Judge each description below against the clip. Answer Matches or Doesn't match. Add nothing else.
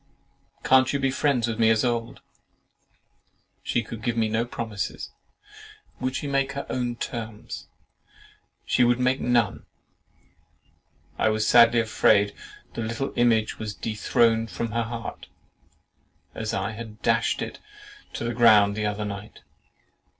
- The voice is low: Matches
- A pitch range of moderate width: Doesn't match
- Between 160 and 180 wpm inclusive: Doesn't match